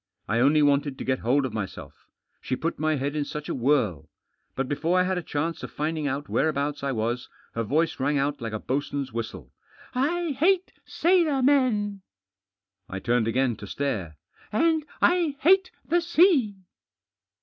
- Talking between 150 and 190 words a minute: Yes, average, 175 wpm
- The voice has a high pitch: No, medium, 145 Hz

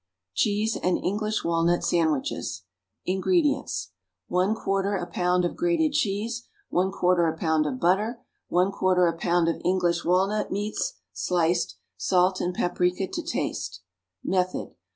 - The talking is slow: Yes, slow, 125 wpm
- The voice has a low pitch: No, medium, 180 Hz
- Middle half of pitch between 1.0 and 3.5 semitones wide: Yes, average, 2.8 semitones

